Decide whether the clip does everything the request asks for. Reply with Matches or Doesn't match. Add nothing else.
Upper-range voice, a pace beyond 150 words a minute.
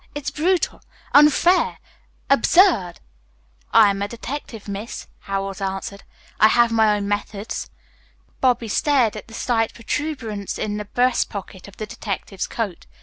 Doesn't match